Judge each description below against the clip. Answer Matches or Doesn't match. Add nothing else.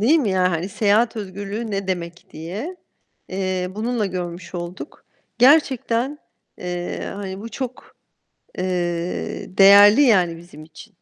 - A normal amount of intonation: Matches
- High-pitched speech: Matches